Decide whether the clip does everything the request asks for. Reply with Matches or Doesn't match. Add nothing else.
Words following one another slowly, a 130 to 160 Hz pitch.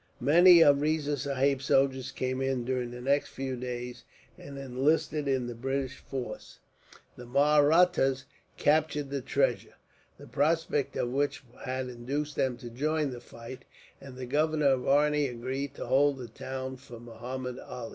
Doesn't match